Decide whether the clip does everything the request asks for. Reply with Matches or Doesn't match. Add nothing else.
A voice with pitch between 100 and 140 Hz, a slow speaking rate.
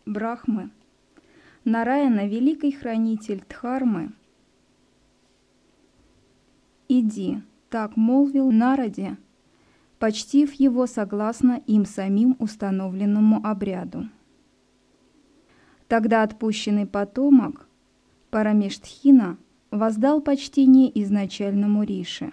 Doesn't match